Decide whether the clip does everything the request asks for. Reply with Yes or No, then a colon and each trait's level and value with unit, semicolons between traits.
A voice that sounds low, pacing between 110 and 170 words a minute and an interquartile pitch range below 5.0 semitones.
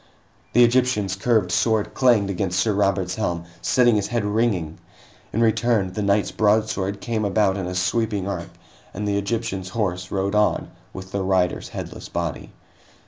Yes: low, 100 Hz; average, 160 wpm; average, 2.8 semitones